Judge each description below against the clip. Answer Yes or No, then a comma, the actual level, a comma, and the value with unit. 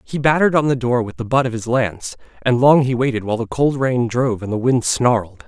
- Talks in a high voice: No, low, 125 Hz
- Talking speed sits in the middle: No, fast, 265 wpm